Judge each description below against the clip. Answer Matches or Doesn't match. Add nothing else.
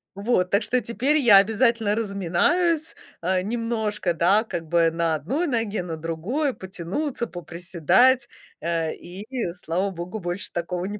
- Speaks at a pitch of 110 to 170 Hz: Doesn't match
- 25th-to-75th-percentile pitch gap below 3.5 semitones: Doesn't match